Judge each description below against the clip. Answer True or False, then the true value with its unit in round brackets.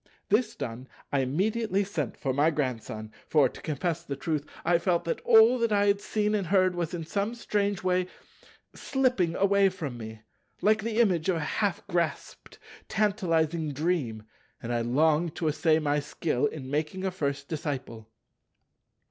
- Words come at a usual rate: True (165 wpm)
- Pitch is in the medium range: True (165 Hz)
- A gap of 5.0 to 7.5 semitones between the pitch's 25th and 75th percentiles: True (5.6 semitones)